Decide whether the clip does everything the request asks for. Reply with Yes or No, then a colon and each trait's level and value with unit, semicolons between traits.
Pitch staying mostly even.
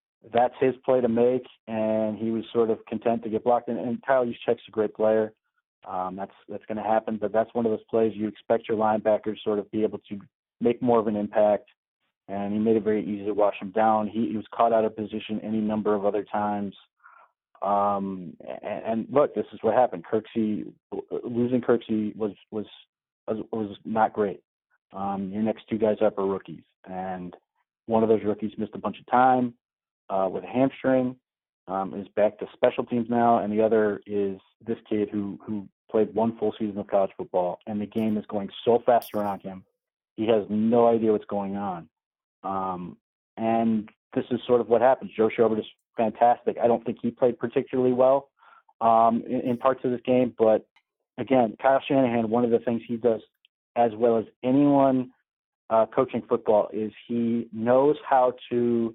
Yes: narrow, 2.2 semitones